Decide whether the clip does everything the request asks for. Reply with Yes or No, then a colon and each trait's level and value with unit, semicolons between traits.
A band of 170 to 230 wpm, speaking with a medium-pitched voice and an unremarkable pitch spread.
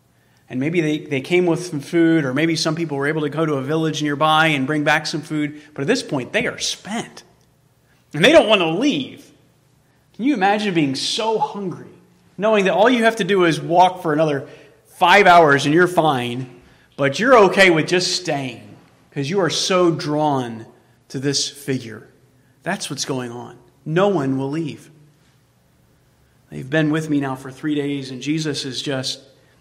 Yes: average, 190 wpm; medium, 150 Hz; average, 4.0 semitones